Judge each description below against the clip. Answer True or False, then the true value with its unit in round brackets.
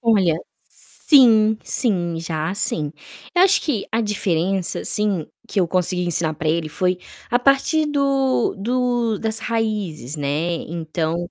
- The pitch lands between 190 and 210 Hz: True (195 Hz)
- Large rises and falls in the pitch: True (6.1 semitones)